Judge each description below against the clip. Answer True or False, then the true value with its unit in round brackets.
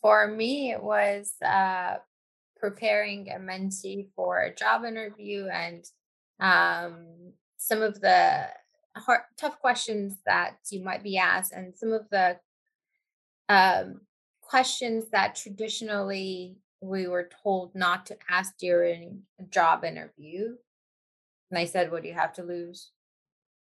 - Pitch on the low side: False (195 Hz)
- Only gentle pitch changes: False (3.6 semitones)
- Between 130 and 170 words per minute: True (135 wpm)